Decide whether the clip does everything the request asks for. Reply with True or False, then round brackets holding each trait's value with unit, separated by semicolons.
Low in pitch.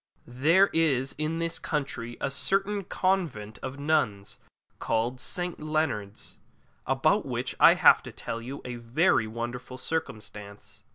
True (130 Hz)